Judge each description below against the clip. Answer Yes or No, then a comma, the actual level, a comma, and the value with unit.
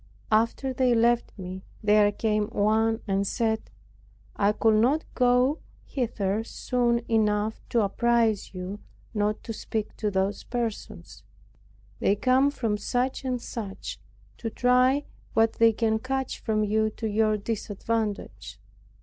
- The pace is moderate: No, slow, 130 wpm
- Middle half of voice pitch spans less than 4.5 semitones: Yes, narrow, 2.4 semitones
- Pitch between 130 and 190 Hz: No, high, 220 Hz